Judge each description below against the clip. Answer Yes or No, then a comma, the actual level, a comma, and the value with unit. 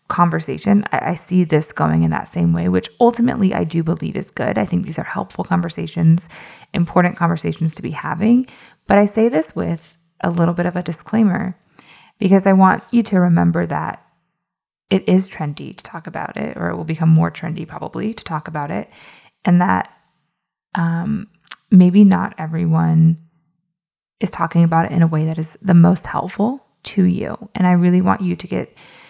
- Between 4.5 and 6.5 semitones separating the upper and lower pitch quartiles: No, average, 3.1 semitones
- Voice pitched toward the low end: No, medium, 170 Hz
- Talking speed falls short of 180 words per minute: No, average, 190 wpm